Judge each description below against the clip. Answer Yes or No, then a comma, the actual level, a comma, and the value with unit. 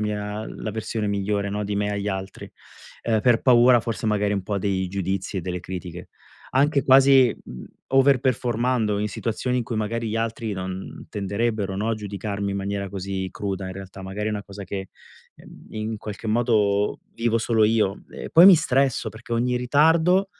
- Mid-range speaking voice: No, low, 105 Hz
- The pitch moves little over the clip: No, average, 3.1 semitones